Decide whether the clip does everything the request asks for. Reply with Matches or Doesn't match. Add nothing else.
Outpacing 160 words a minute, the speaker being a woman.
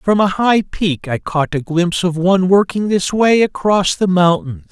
Doesn't match